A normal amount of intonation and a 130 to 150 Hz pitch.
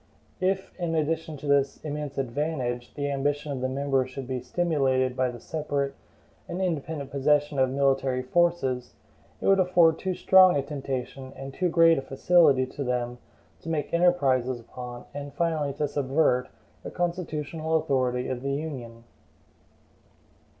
Yes: average, 3.7 semitones; medium, 140 Hz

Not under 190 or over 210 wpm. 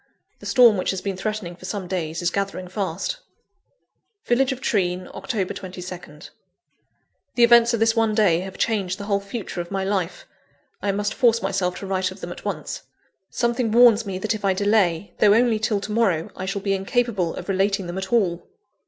Yes: average, 195 wpm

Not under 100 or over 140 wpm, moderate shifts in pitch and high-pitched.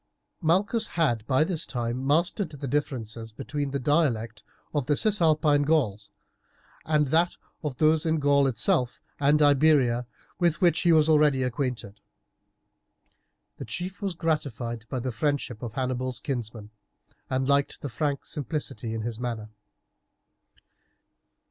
No: slow, 135 wpm; average, 4.4 semitones; medium, 140 Hz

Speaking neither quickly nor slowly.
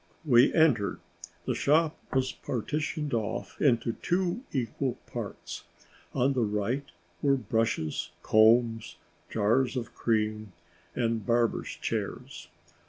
No: slow, 105 wpm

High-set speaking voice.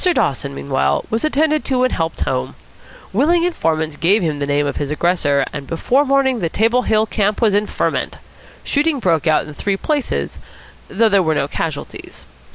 Yes: high, 195 Hz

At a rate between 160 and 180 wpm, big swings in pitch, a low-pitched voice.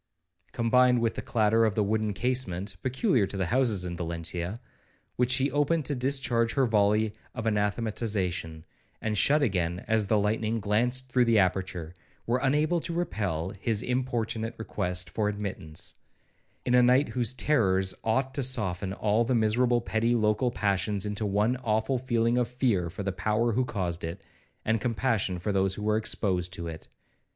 No: average, 170 wpm; average, 4.1 semitones; low, 110 Hz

